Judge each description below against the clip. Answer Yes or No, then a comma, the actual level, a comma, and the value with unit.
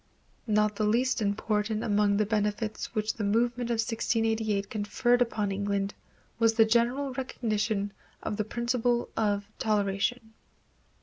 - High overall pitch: Yes, high, 220 Hz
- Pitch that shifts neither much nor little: No, narrow, 2.3 semitones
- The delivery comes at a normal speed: No, slow, 130 wpm